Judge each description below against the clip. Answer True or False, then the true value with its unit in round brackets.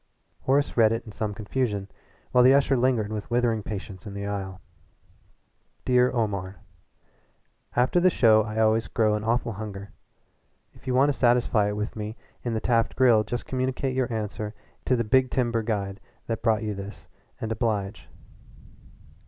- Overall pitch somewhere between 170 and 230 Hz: False (110 Hz)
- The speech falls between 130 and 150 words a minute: False (165 wpm)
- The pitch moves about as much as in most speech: True (3.0 semitones)